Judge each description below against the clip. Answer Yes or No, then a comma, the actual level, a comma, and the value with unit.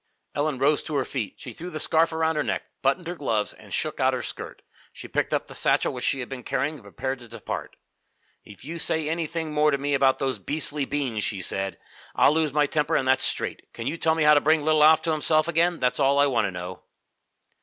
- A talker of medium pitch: Yes, medium, 145 Hz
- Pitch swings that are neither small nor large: Yes, average, 3.1 semitones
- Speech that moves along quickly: Yes, fast, 245 wpm